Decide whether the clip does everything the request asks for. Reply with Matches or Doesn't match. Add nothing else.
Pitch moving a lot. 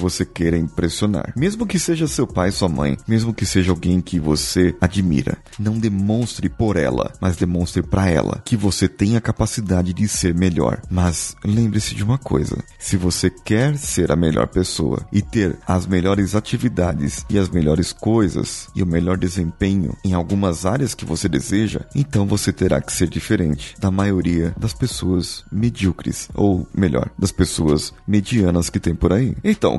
Doesn't match